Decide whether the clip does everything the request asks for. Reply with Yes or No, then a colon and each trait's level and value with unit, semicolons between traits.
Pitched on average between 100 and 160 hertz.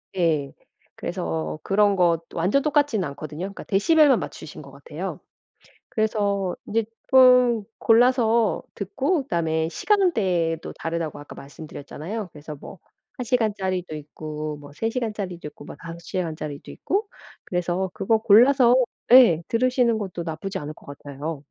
No: medium, 185 Hz